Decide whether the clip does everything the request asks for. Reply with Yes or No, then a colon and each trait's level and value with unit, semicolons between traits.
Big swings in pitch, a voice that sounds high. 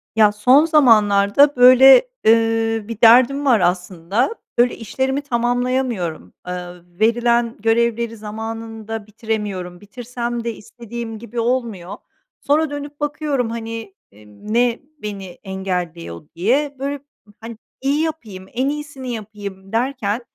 No: average, 3.6 semitones; high, 230 Hz